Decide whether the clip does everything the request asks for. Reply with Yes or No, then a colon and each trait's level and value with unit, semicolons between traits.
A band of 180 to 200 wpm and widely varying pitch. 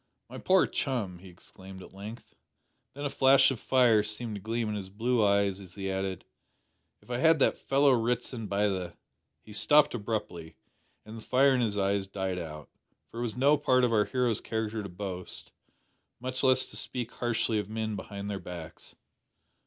No: average, 190 wpm; average, 4.2 semitones